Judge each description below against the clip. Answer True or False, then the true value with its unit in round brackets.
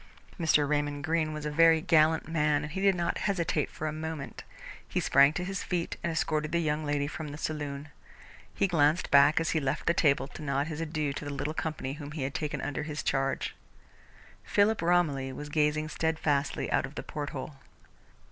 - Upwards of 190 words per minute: True (200 wpm)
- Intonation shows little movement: True (2.0 semitones)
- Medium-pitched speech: True (150 Hz)